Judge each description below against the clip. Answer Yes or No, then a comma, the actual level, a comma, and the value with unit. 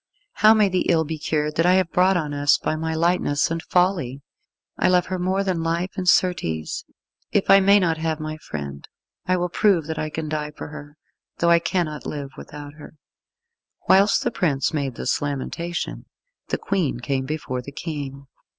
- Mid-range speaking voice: Yes, medium, 160 Hz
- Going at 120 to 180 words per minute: No, average, 190 wpm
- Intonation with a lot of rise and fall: No, average, 3.7 semitones